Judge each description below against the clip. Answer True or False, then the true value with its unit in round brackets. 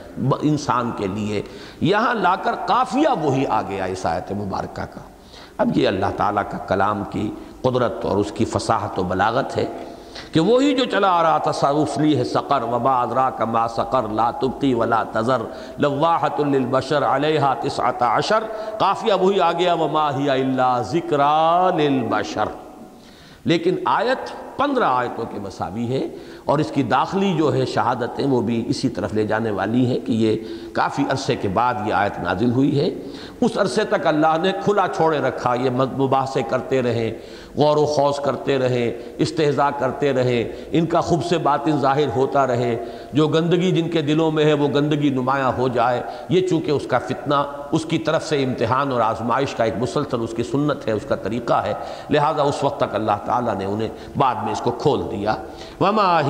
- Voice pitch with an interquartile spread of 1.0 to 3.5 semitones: False (4.2 semitones)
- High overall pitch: False (140 Hz)